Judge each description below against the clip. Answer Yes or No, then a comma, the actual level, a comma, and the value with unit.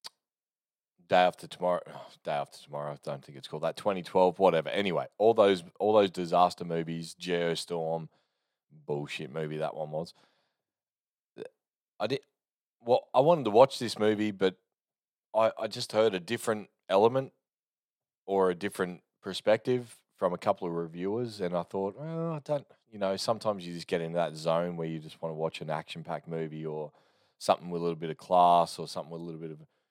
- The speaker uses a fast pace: No, average, 185 wpm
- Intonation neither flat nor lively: Yes, average, 4.5 semitones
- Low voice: Yes, very low, 90 Hz